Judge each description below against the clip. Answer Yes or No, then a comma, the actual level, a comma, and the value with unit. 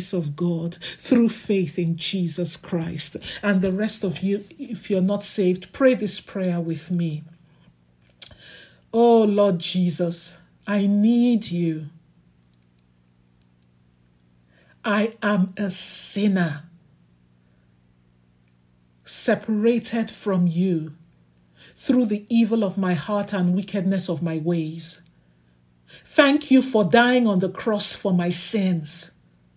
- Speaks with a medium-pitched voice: Yes, medium, 175 Hz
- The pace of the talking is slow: Yes, slow, 110 wpm